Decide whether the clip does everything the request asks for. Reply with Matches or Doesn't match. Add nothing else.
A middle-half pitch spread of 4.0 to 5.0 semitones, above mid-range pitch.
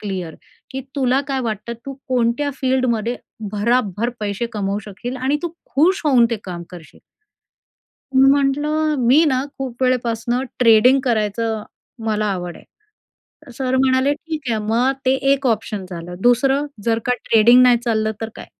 Doesn't match